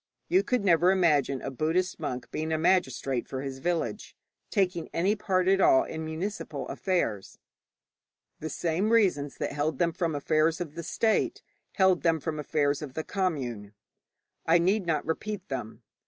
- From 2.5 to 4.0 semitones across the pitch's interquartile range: No, average, 4.4 semitones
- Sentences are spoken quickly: No, average, 165 wpm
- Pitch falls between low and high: Yes, medium, 165 Hz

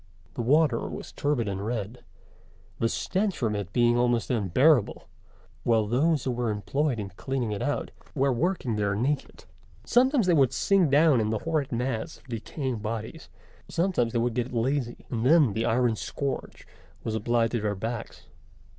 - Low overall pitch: Yes, low, 120 Hz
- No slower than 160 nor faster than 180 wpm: Yes, average, 170 wpm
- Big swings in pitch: No, average, 4.4 semitones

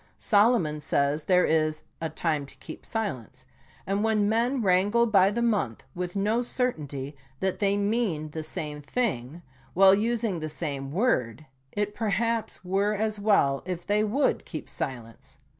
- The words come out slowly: No, average, 160 wpm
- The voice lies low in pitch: No, high, 195 Hz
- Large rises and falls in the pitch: Yes, wide, 6.0 semitones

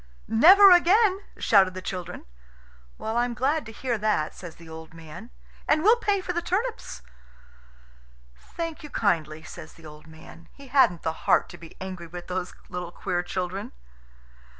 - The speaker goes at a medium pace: Yes, average, 160 wpm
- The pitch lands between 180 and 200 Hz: Yes, high, 190 Hz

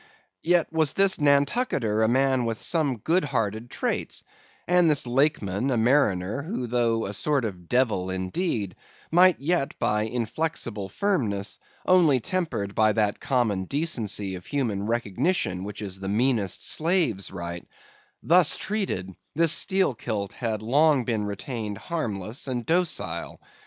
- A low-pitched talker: Yes, low, 120 Hz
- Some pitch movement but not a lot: No, wide, 7.2 semitones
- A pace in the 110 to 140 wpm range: Yes, slow, 135 wpm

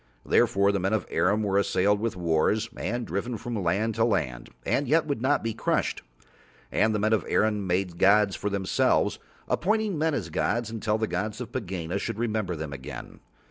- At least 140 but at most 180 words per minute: No, average, 195 wpm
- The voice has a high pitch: No, low, 105 Hz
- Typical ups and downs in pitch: Yes, average, 3.2 semitones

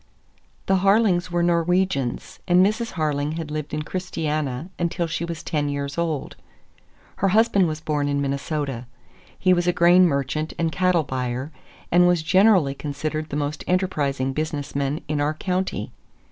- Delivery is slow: No, average, 160 wpm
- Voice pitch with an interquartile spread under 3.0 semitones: No, average, 3.7 semitones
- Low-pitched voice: No, medium, 155 Hz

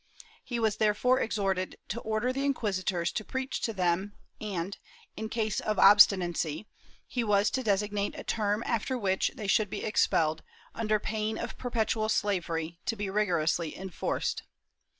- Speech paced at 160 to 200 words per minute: No, average, 150 wpm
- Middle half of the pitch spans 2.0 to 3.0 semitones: Yes, average, 2.7 semitones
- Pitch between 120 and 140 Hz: No, high, 210 Hz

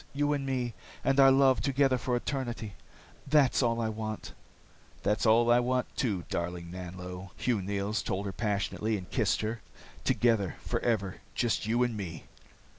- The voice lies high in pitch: No, low, 115 Hz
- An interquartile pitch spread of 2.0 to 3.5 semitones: No, average, 4.2 semitones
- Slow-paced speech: No, average, 160 wpm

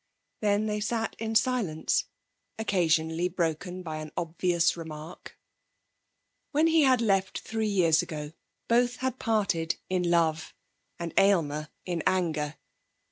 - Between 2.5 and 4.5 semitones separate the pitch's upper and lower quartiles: No, average, 5.1 semitones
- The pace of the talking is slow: Yes, slow, 125 wpm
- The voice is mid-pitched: Yes, medium, 180 Hz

